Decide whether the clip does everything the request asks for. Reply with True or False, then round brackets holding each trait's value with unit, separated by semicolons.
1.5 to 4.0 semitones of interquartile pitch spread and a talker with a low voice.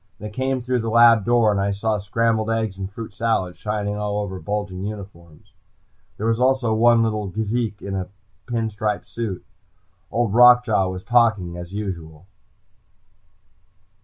True (2.8 semitones; 105 Hz)